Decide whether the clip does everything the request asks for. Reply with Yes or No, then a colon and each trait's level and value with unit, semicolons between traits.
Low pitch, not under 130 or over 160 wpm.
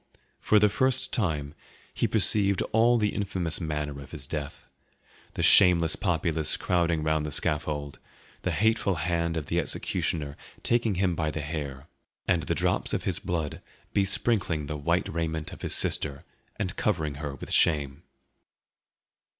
Yes: very low, 80 Hz; average, 150 wpm